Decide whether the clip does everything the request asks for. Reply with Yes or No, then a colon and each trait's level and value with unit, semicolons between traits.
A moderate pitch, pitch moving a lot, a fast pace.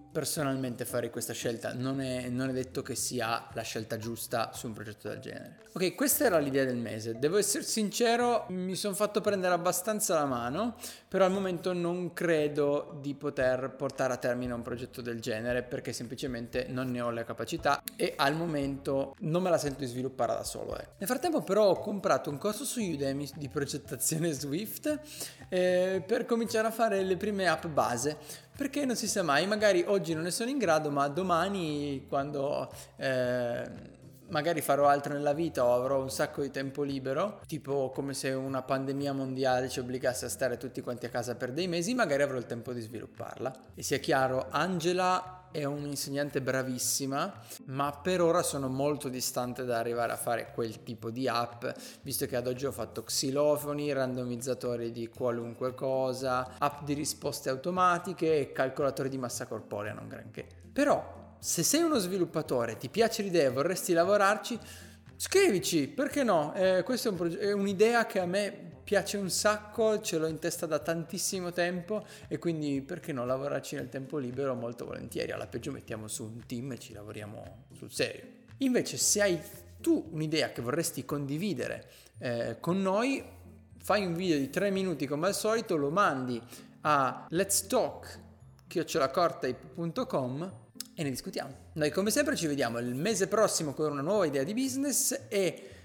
Yes: medium, 145 Hz; wide, 6.4 semitones; fast, 175 wpm